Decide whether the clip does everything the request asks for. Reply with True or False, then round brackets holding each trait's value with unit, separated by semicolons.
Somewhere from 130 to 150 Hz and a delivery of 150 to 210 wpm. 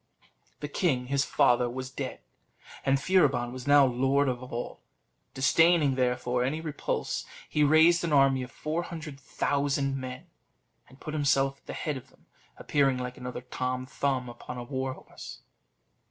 True (135 Hz; 160 wpm)